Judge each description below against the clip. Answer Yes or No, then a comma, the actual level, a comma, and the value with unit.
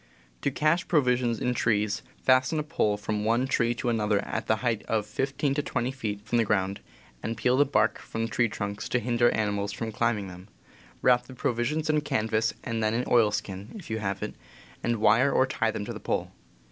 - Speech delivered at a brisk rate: Yes, fast, 210 wpm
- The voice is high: No, low, 115 Hz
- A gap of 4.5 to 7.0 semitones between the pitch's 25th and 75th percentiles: No, average, 3.3 semitones